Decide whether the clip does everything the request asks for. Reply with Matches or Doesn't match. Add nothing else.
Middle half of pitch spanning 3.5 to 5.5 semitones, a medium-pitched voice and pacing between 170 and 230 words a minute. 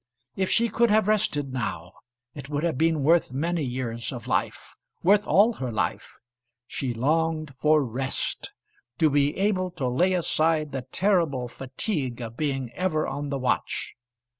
Doesn't match